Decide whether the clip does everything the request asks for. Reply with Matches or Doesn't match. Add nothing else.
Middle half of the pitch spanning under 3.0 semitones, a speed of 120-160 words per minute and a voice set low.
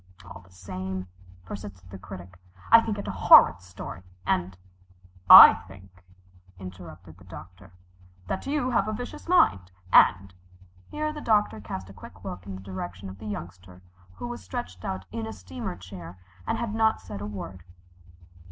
Doesn't match